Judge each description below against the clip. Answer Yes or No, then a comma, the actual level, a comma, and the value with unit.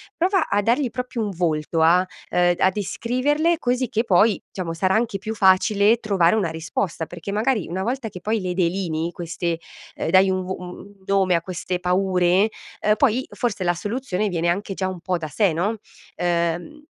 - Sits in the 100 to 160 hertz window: No, high, 190 Hz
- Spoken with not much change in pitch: No, average, 3.9 semitones